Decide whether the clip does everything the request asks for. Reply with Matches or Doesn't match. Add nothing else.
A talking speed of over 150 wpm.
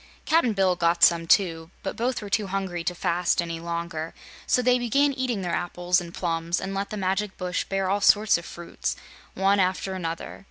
Matches